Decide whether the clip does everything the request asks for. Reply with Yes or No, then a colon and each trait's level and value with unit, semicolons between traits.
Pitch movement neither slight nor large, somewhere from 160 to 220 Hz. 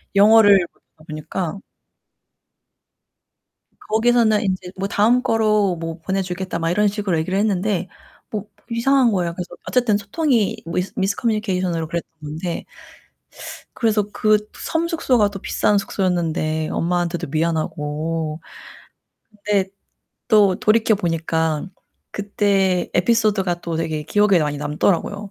Yes: average, 4.1 semitones; high, 190 Hz